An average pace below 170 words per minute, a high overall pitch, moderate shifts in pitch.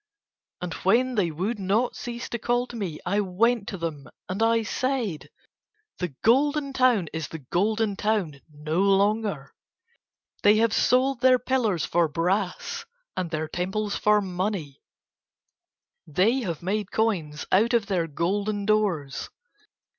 Yes: average, 140 wpm; high, 205 Hz; average, 4.9 semitones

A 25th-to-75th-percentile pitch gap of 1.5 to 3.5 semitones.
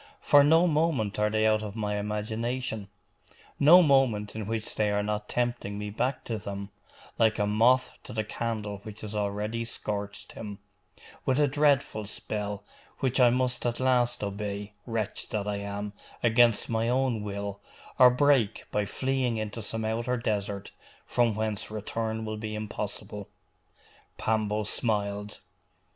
Yes: average, 2.8 semitones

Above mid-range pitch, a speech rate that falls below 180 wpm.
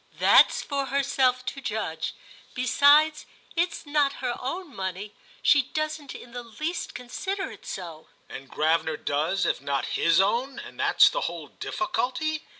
Yes: very high, 255 Hz; average, 150 wpm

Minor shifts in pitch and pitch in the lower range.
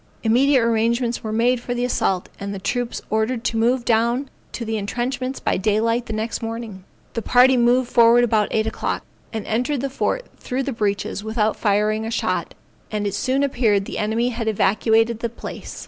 No: narrow, 2.1 semitones; high, 230 Hz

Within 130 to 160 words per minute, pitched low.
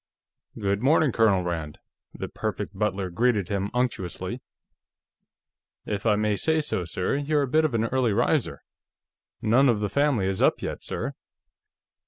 Yes: average, 155 wpm; low, 110 Hz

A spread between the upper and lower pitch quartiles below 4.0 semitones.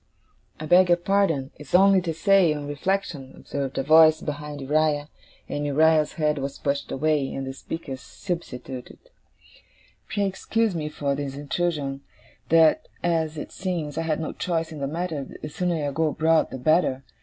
Yes: average, 3.2 semitones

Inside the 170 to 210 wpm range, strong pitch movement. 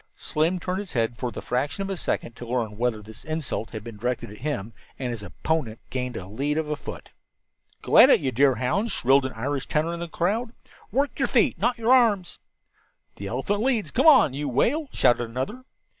Yes: fast, 205 wpm; wide, 7.9 semitones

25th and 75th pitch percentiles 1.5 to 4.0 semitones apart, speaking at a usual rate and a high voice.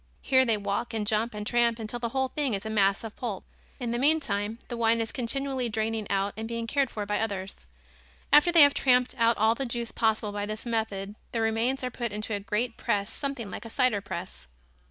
No: average, 2.9 semitones; fast, 225 wpm; high, 225 Hz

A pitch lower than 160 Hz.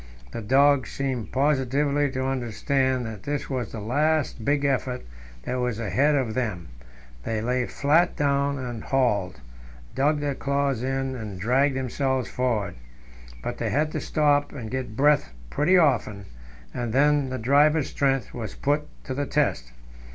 Yes: low, 135 Hz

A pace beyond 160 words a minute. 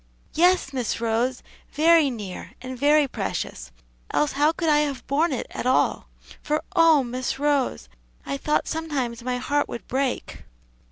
No: average, 155 wpm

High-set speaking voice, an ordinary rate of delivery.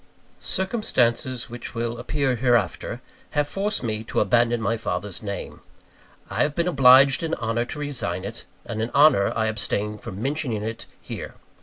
No: low, 120 Hz; average, 160 wpm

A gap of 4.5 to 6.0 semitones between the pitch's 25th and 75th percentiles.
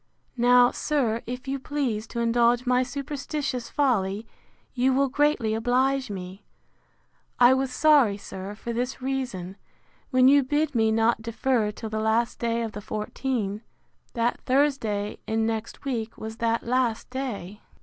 No: average, 3.3 semitones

